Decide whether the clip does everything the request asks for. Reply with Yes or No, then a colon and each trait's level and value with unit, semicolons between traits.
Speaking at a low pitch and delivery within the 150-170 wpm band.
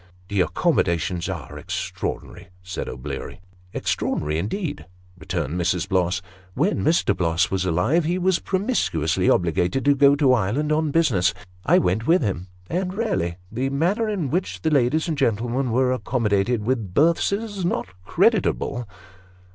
Yes: low, 120 Hz; average, 155 wpm